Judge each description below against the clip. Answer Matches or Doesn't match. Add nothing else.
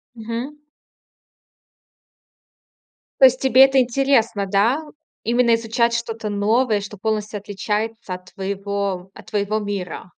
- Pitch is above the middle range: Matches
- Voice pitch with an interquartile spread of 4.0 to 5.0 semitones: Doesn't match